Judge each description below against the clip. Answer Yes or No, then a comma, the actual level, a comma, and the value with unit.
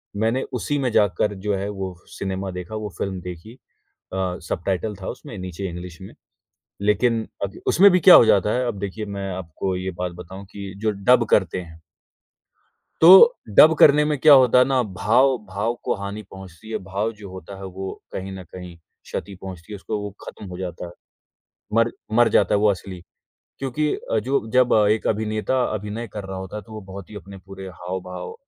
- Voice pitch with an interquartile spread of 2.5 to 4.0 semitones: Yes, average, 3.2 semitones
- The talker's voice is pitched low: Yes, low, 100 Hz